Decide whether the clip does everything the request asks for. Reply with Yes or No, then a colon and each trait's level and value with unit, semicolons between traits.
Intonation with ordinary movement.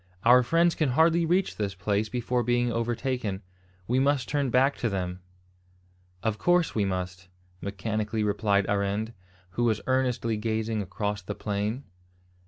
Yes: average, 3.7 semitones